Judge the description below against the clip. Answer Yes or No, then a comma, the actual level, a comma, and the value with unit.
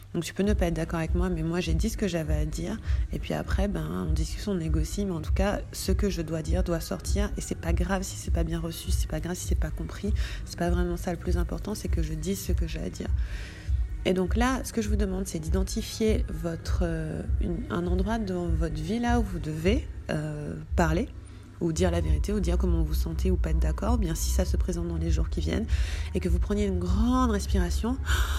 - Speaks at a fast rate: Yes, fast, 275 wpm